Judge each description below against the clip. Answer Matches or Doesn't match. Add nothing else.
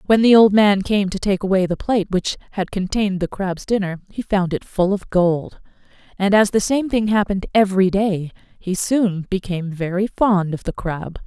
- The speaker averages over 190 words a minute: Matches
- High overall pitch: Matches